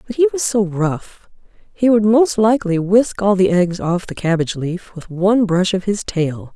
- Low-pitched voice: No, high, 195 Hz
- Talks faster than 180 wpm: Yes, average, 200 wpm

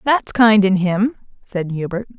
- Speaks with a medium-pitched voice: No, high, 205 Hz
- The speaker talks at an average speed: Yes, average, 165 wpm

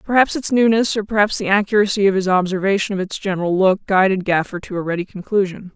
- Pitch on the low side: No, high, 195 Hz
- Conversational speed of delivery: No, fast, 210 wpm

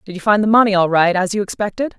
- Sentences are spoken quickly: Yes, fast, 300 wpm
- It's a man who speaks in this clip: No, female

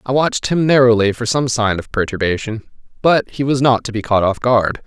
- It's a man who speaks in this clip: Yes, male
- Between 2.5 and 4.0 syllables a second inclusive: No, 5.5 syllables/s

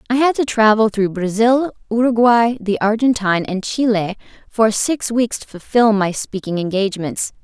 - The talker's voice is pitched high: Yes, high, 220 Hz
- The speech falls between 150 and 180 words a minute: Yes, average, 155 wpm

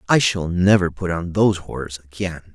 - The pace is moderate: Yes, average, 190 wpm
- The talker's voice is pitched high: No, very low, 90 Hz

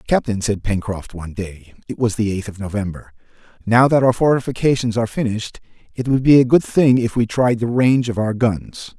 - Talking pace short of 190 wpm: No, fast, 205 wpm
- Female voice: No, male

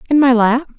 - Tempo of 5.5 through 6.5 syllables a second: No, 5.3 syllables/s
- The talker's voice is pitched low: No, very high, 255 Hz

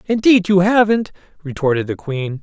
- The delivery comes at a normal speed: Yes, average, 150 wpm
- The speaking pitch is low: No, medium, 175 Hz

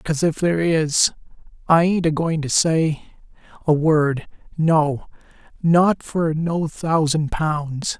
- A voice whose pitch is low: No, medium, 160 Hz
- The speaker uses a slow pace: Yes, slow, 130 wpm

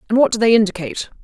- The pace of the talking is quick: Yes, fast, 245 wpm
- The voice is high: Yes, high, 220 Hz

